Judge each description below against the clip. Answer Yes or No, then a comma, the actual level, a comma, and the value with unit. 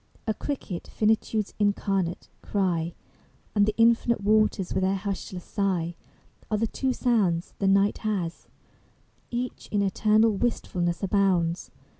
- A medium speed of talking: No, slow, 125 wpm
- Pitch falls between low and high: No, high, 200 Hz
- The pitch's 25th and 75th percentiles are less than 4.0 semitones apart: Yes, average, 2.8 semitones